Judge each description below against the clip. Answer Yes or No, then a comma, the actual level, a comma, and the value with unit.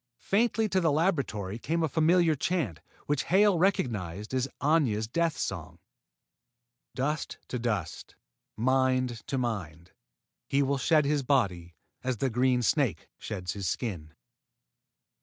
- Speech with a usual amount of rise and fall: No, wide, 7.0 semitones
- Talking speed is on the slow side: Yes, slow, 130 wpm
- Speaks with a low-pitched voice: Yes, low, 130 Hz